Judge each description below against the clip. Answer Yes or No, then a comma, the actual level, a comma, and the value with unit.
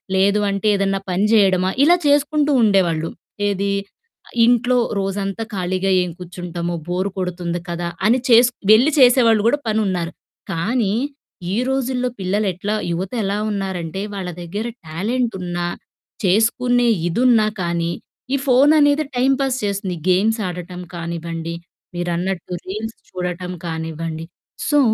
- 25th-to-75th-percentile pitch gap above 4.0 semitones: Yes, average, 4.7 semitones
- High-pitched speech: Yes, high, 195 Hz